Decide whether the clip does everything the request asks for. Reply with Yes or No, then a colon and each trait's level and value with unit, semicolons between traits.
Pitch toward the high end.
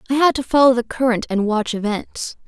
Yes: high, 240 Hz